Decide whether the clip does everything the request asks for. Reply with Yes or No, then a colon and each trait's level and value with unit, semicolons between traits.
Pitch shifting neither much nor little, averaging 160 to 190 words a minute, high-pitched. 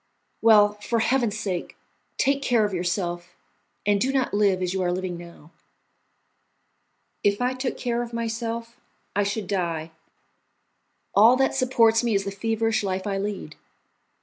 No: average, 3.7 semitones; average, 150 wpm; high, 210 Hz